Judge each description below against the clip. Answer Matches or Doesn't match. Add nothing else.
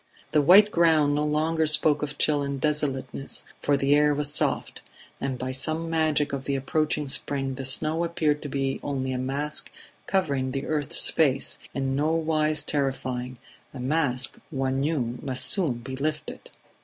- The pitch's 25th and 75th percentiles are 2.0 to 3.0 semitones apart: Matches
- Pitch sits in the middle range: Matches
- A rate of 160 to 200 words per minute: Matches